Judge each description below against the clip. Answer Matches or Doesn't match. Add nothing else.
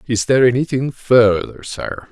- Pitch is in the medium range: Doesn't match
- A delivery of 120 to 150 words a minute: Matches